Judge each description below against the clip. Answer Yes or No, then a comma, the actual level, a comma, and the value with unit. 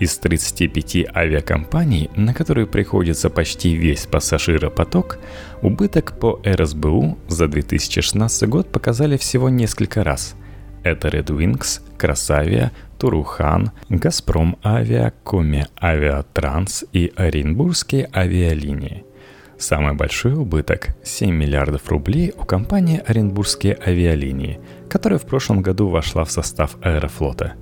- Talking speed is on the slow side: Yes, slow, 105 wpm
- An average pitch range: No, wide, 6.1 semitones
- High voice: No, very low, 90 Hz